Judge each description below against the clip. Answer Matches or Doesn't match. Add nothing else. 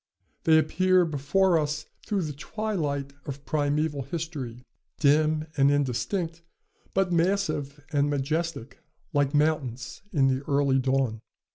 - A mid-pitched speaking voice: Matches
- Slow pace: Matches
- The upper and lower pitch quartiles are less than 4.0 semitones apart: Matches